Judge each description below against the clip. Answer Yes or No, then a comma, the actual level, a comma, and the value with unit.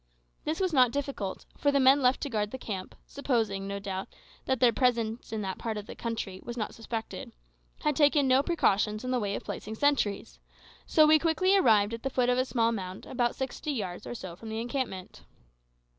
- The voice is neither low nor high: No, high, 235 Hz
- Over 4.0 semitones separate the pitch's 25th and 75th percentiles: Yes, average, 4.5 semitones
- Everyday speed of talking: No, fast, 210 wpm